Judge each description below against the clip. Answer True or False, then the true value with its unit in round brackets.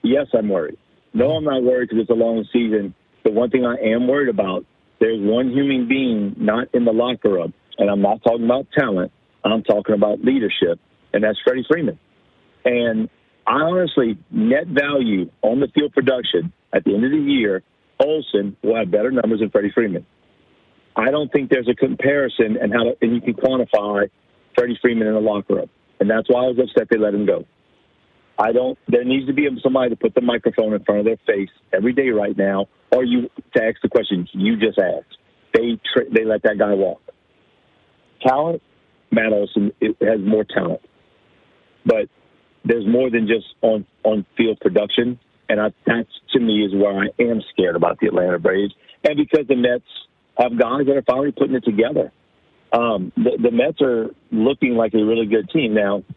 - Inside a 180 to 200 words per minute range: True (195 wpm)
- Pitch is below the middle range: True (115 Hz)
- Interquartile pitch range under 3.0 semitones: False (3.5 semitones)